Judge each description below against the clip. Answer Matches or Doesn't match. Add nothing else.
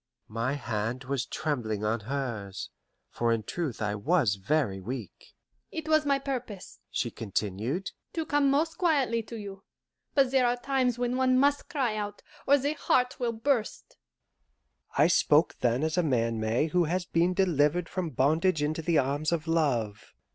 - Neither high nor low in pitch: Matches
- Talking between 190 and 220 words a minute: Doesn't match